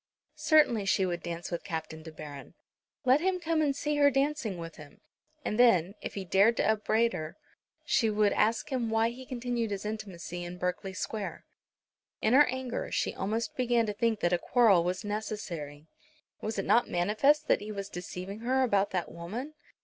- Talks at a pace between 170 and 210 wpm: Yes, average, 190 wpm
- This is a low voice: No, high, 215 Hz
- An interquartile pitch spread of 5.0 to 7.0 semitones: Yes, average, 5.3 semitones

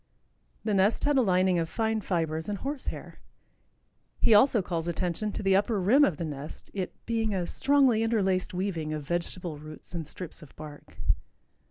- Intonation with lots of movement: No, average, 4.9 semitones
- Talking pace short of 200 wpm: Yes, average, 180 wpm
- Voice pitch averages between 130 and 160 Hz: No, medium, 185 Hz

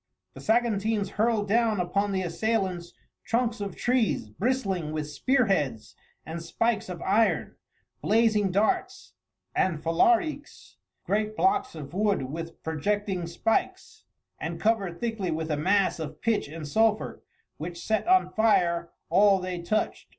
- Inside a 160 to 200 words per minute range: No, slow, 135 wpm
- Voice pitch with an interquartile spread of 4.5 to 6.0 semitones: Yes, average, 4.8 semitones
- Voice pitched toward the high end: Yes, high, 200 Hz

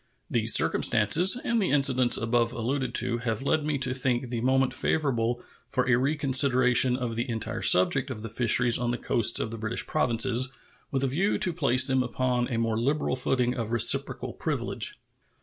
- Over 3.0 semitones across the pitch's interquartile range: No, narrow, 2.4 semitones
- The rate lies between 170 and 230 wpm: Yes, average, 185 wpm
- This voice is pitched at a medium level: No, low, 125 Hz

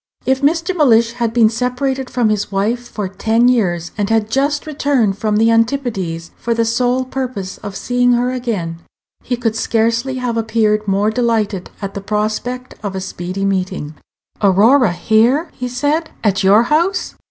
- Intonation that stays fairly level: No, average, 3.7 semitones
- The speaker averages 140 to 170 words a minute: Yes, average, 165 wpm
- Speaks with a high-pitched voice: Yes, high, 230 Hz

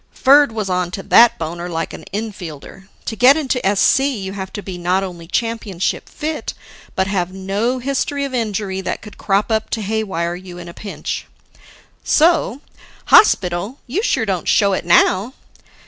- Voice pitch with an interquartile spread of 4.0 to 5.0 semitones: Yes, average, 4.5 semitones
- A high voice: Yes, high, 200 Hz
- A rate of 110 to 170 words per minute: Yes, average, 165 wpm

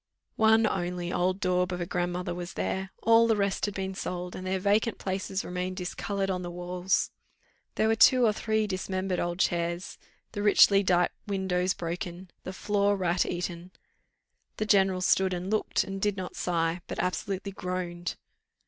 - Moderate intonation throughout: No, narrow, 2.0 semitones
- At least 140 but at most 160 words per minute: No, average, 170 wpm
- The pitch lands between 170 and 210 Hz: Yes, medium, 185 Hz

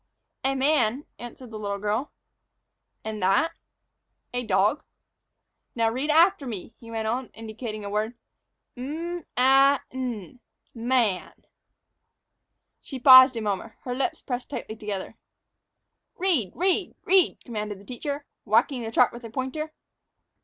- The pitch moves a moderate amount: Yes, average, 4.1 semitones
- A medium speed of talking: No, slow, 130 wpm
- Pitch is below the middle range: No, high, 245 Hz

